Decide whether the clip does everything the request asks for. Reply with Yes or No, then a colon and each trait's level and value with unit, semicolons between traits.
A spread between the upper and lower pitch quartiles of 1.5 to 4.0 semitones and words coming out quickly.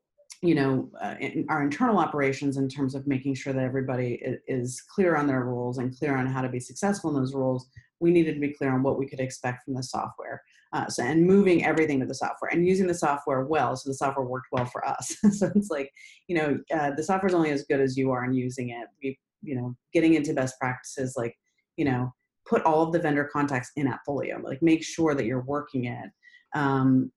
Yes: average, 3.6 semitones; fast, 235 wpm